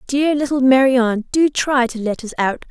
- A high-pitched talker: Yes, very high, 255 Hz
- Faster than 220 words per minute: No, average, 200 wpm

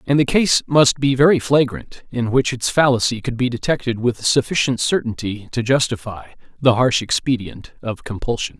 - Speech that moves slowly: No, average, 165 wpm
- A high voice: No, low, 125 Hz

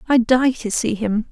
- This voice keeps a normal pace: No, fast, 230 wpm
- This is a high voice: Yes, high, 235 Hz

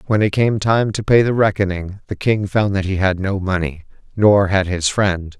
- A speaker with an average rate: No, fast, 225 wpm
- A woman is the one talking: No, male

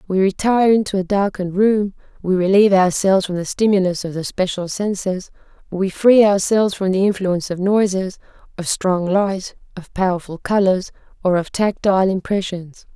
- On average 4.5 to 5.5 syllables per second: Yes, 5.3 syllables/s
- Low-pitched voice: No, high, 190 Hz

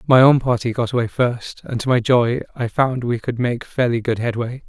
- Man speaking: Yes, male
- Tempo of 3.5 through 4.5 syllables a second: No, 5.1 syllables/s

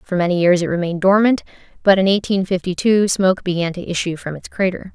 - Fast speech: Yes, fast, 220 wpm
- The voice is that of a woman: Yes, female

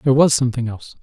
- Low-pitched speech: Yes, low, 125 Hz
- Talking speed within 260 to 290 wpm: No, fast, 235 wpm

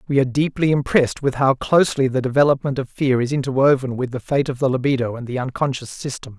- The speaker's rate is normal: No, fast, 215 wpm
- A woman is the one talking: No, male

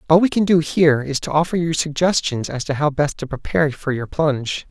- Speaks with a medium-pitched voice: Yes, medium, 150 Hz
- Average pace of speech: No, fast, 245 wpm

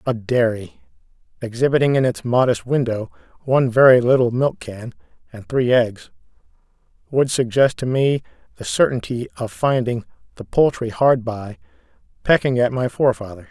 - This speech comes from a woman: No, male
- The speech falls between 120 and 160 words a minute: Yes, average, 140 wpm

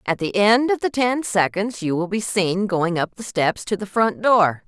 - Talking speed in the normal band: No, fast, 245 wpm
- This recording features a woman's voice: Yes, female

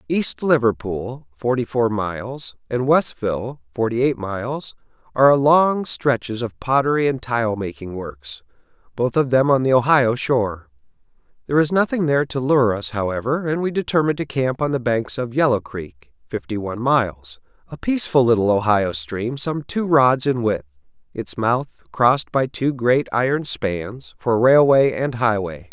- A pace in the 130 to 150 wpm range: No, average, 165 wpm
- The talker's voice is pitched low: Yes, low, 120 Hz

